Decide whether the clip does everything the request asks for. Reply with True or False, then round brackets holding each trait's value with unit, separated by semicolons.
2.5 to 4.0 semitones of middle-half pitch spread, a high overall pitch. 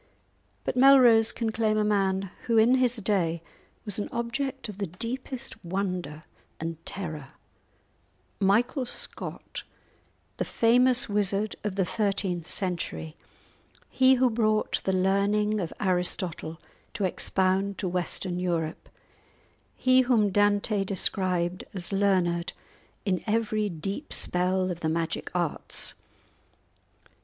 True (3.7 semitones; 195 Hz)